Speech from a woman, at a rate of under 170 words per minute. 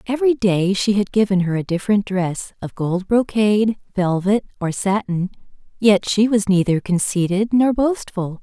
Yes: female; average, 155 wpm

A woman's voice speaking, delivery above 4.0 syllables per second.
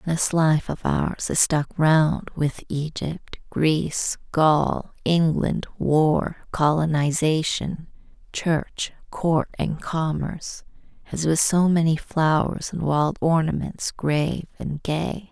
No: female; 3.3 syllables/s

